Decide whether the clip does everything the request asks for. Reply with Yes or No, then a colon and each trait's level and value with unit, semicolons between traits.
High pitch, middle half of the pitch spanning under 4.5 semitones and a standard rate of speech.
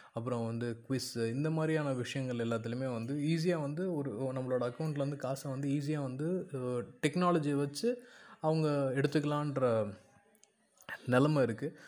No: medium, 140 Hz; average, 3.6 semitones; average, 115 wpm